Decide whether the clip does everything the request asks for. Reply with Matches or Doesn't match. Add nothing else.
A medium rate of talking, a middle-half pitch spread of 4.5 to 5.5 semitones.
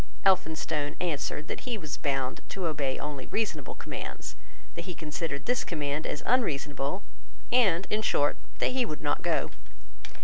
Matches